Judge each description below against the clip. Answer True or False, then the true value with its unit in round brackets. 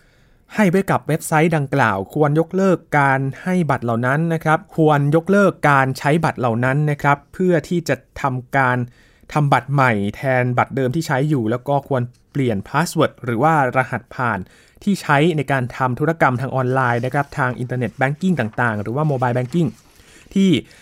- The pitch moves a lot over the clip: False (4.0 semitones)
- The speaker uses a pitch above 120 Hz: True (140 Hz)